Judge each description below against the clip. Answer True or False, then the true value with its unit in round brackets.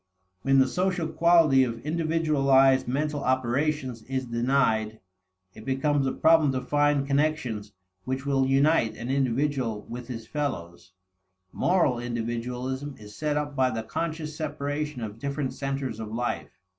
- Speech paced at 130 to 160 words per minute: True (140 wpm)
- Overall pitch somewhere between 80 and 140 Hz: True (135 Hz)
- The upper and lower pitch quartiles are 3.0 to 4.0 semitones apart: True (3.6 semitones)